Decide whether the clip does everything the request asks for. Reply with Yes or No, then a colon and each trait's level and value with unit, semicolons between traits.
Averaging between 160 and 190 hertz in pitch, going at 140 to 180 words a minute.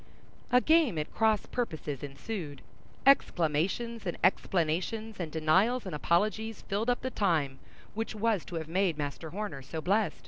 Yes: medium, 185 Hz; average, 150 wpm